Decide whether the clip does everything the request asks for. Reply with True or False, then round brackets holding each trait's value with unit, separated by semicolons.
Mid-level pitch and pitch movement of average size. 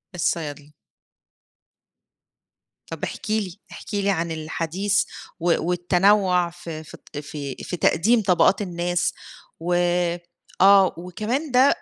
True (180 Hz; 3.3 semitones)